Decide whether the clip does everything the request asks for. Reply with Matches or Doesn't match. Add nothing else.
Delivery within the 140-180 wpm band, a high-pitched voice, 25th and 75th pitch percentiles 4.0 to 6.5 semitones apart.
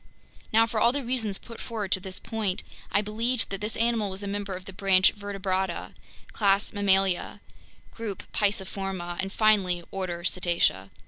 Doesn't match